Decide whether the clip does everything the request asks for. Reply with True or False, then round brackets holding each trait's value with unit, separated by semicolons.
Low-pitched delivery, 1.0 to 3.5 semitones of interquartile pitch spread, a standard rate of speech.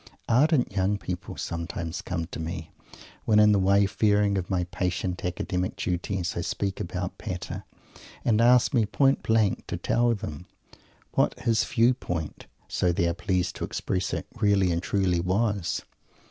True (95 Hz; 3.2 semitones; 160 wpm)